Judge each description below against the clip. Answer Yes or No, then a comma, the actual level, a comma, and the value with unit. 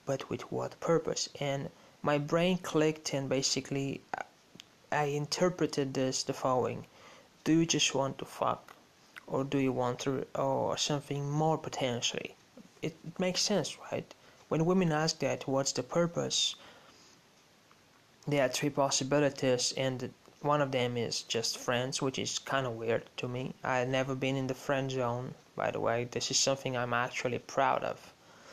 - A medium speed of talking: Yes, average, 160 wpm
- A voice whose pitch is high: No, low, 135 Hz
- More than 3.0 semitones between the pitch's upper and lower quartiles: No, narrow, 2.4 semitones